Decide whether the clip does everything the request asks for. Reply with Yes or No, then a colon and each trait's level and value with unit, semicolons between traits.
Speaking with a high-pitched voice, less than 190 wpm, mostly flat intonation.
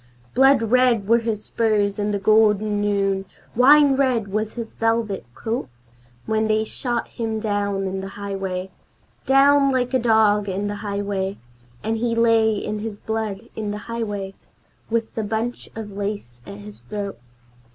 Yes: high, 215 Hz; average, 160 wpm; narrow, 2.3 semitones